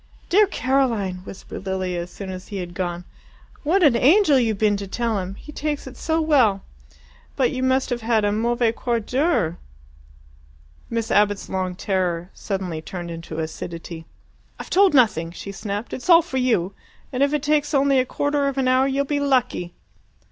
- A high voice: Yes, high, 230 Hz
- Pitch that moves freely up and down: Yes, wide, 6.5 semitones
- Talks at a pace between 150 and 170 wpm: No, average, 185 wpm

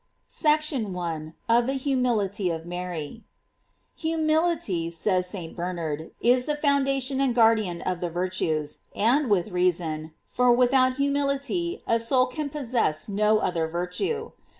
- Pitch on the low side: No, high, 225 Hz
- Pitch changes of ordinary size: No, wide, 7.5 semitones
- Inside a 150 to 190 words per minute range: No, slow, 135 wpm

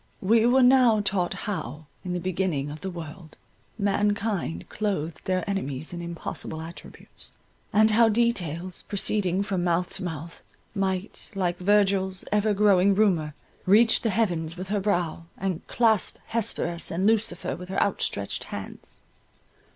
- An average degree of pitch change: Yes, average, 3.4 semitones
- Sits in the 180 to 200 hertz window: Yes, high, 190 Hz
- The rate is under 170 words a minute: Yes, average, 140 wpm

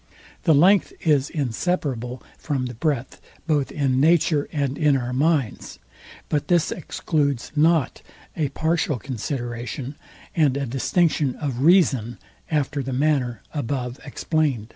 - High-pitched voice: No, medium, 140 Hz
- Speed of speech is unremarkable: No, slow, 125 wpm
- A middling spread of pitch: Yes, average, 3.6 semitones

